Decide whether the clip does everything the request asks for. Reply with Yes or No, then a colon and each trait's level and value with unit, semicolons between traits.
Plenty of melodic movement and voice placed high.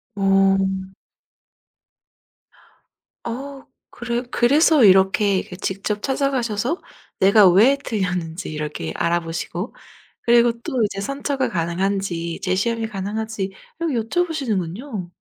No: average, 4.4 semitones; high, 205 Hz